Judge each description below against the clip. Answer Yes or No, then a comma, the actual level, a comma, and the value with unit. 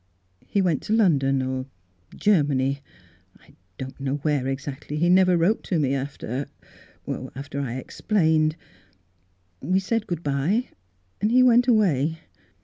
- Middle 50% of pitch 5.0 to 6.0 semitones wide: Yes, wide, 5.6 semitones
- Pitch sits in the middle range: Yes, medium, 145 Hz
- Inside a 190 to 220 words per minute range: No, average, 155 wpm